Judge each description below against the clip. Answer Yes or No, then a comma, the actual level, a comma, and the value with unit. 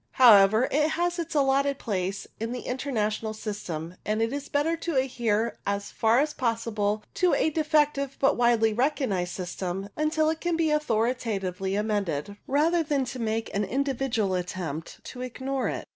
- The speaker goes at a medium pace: Yes, average, 165 wpm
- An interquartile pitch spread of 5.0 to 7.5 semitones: Yes, wide, 5.5 semitones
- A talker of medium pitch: No, high, 235 Hz